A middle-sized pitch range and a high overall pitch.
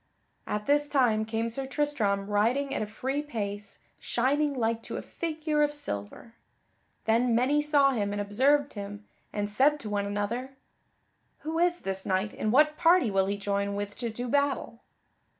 No: wide, 5.8 semitones; high, 235 Hz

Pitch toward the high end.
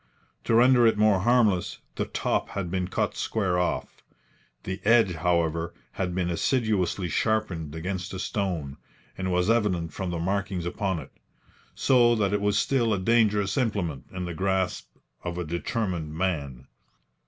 No: very low, 95 Hz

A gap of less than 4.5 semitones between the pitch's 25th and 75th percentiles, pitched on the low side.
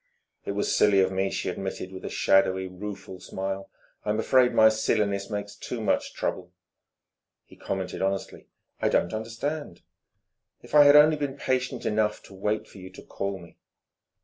Yes: average, 2.8 semitones; low, 100 Hz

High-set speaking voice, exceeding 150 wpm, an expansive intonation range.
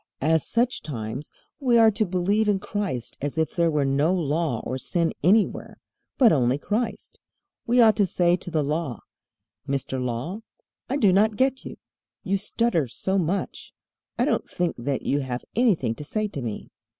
No: medium, 175 Hz; average, 175 wpm; wide, 7.4 semitones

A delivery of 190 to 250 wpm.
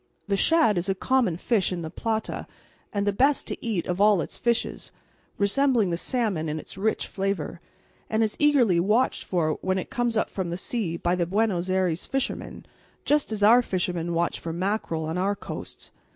Yes: average, 195 wpm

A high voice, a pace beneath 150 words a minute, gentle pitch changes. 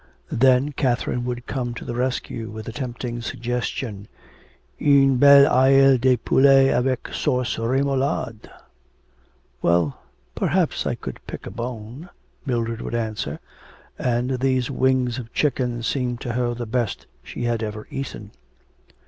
No: low, 125 Hz; slow, 135 wpm; narrow, 2.2 semitones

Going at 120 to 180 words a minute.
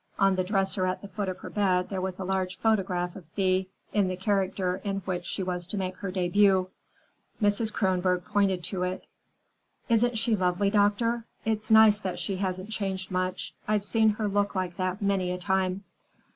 No: average, 190 wpm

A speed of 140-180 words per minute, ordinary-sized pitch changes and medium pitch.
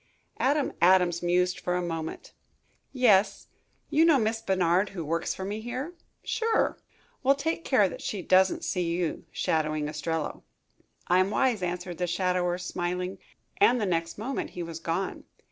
Yes: average, 155 wpm; average, 4.2 semitones; medium, 180 Hz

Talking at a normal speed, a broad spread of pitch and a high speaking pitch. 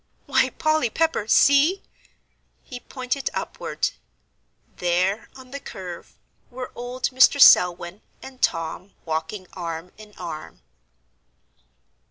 No: slow, 105 wpm; wide, 6.8 semitones; high, 215 Hz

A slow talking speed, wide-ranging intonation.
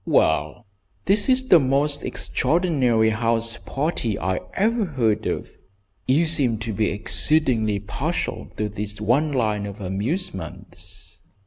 Yes: slow, 125 wpm; wide, 6.5 semitones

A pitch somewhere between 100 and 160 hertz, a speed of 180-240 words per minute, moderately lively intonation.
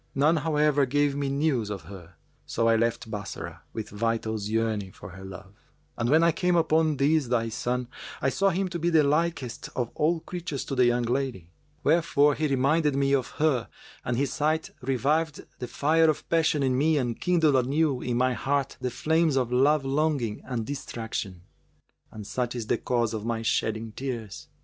Yes: low, 135 Hz; average, 190 wpm; average, 4.8 semitones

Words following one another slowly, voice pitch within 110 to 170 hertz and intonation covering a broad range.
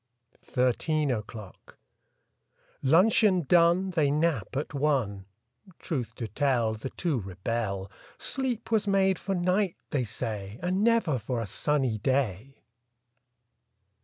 Yes: slow, 125 wpm; medium, 140 Hz; wide, 7.9 semitones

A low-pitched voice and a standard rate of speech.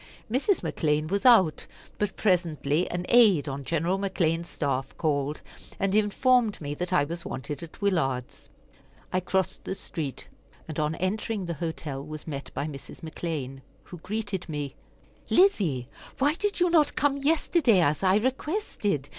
No: medium, 175 Hz; average, 155 wpm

